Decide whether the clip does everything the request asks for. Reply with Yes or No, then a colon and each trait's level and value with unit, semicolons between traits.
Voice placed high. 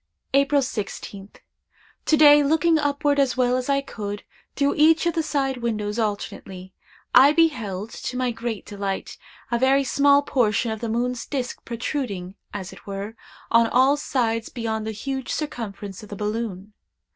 Yes: high, 240 Hz